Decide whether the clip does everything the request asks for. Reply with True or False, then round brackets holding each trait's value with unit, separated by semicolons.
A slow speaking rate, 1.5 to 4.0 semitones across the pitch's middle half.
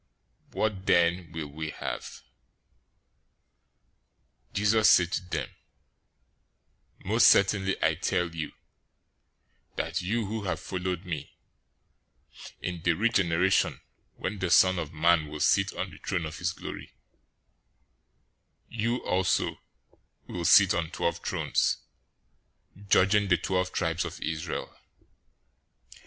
True (115 wpm; 2.8 semitones)